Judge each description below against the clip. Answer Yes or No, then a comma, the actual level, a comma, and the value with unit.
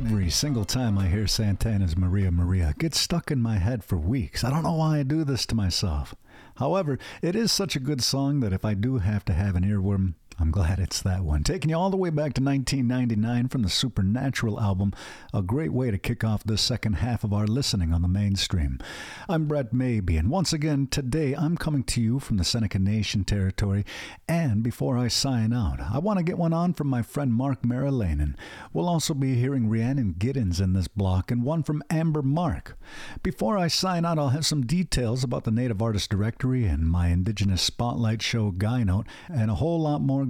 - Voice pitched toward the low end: Yes, low, 120 Hz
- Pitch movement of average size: No, wide, 5.8 semitones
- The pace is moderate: No, fast, 215 wpm